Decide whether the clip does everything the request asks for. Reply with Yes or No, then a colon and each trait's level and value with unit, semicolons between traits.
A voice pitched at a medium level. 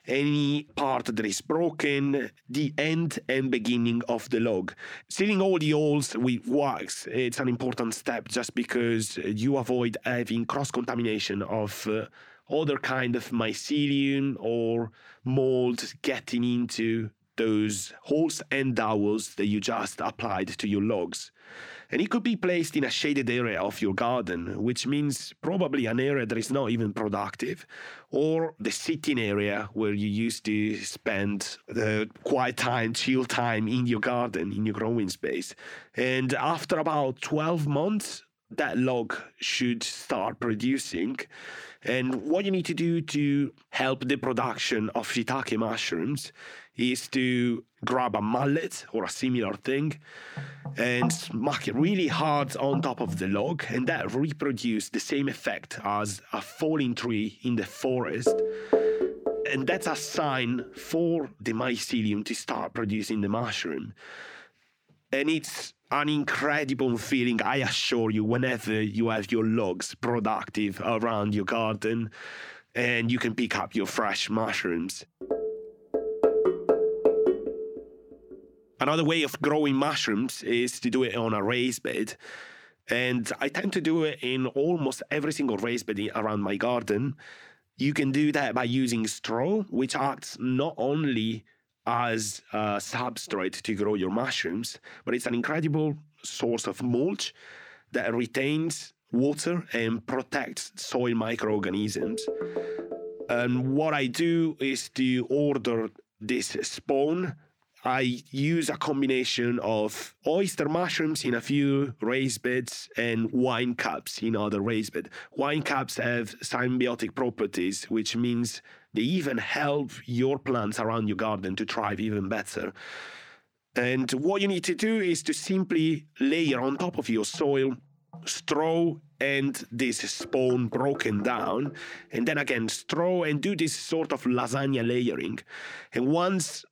No: low, 125 Hz